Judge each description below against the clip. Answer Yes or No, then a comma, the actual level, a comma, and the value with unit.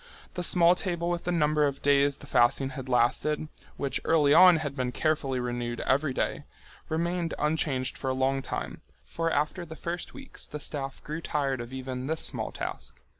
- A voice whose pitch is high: No, medium, 145 Hz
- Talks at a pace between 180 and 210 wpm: Yes, average, 185 wpm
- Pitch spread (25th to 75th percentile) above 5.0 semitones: No, average, 3.8 semitones